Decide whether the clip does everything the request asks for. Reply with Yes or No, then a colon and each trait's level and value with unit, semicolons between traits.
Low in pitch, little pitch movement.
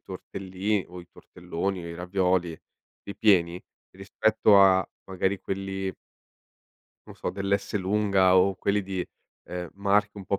Yes: very low, 95 Hz; narrow, 1.4 semitones